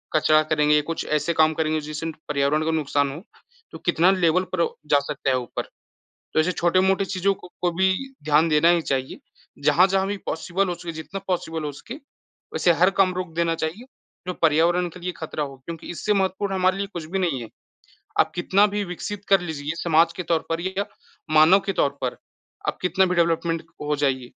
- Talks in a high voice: No, medium, 170 Hz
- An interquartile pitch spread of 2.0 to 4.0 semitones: Yes, average, 3.0 semitones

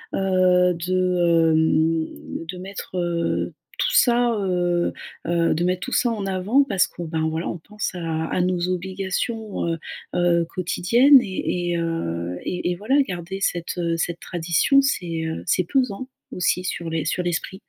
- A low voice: No, medium, 180 Hz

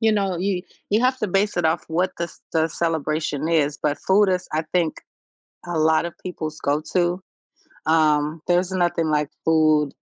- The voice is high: No, medium, 165 Hz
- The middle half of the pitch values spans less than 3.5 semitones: Yes, average, 2.9 semitones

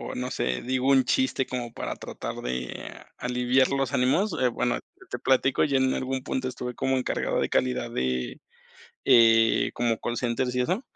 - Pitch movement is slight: Yes, narrow, 1.9 semitones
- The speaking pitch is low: Yes, low, 125 Hz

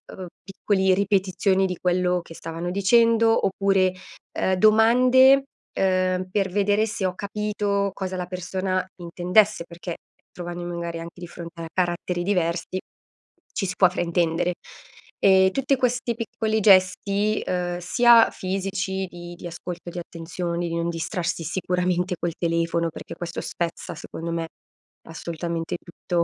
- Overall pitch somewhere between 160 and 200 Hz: Yes, medium, 185 Hz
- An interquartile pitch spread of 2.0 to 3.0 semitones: Yes, narrow, 2.4 semitones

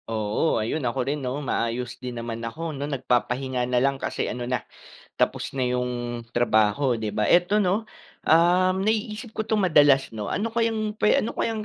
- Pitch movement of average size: No, wide, 7.3 semitones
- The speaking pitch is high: No, low, 135 Hz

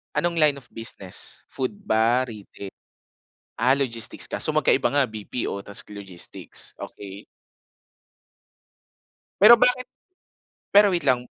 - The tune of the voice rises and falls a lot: Yes, wide, 6.8 semitones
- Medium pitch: No, low, 125 Hz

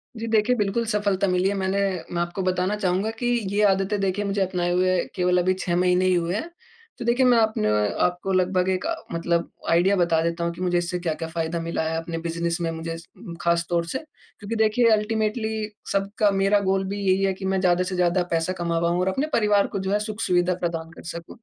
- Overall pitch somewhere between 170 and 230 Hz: Yes, medium, 185 Hz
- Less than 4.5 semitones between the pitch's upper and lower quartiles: Yes, average, 3.0 semitones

